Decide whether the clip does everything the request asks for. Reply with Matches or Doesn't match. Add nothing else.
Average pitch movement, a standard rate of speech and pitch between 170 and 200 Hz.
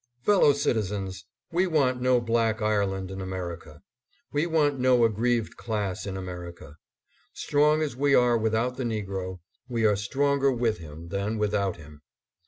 Doesn't match